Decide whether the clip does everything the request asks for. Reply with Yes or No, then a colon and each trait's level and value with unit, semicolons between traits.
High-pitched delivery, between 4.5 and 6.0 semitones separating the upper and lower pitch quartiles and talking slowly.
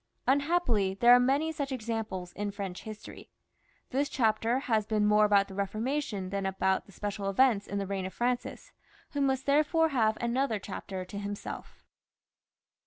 No: high, 215 Hz; average, 4.8 semitones; average, 165 wpm